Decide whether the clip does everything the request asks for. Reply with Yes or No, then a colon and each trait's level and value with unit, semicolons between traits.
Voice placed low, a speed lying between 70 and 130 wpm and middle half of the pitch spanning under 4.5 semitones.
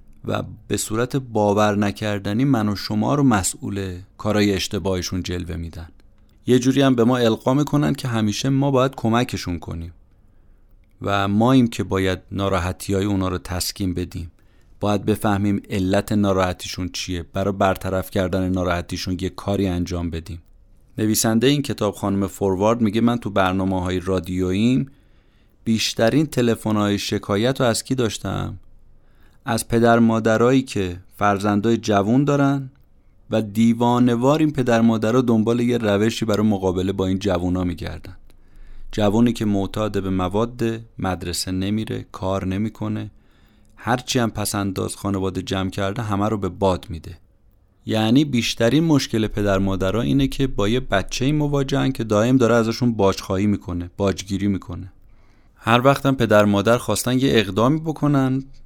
No: low, 105 Hz; average, 145 wpm; average, 3.5 semitones